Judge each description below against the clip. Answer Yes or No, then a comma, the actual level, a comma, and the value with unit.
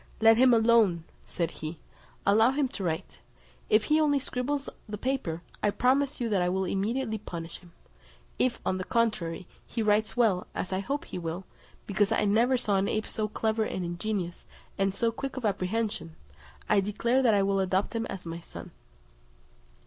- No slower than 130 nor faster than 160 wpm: No, average, 185 wpm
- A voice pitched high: Yes, high, 210 Hz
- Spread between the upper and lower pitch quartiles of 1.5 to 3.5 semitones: No, average, 4.0 semitones